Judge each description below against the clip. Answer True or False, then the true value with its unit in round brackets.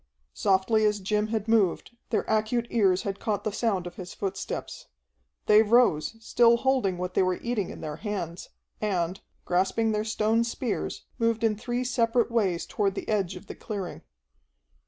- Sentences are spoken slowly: False (170 wpm)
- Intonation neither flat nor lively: True (3.2 semitones)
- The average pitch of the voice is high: True (210 Hz)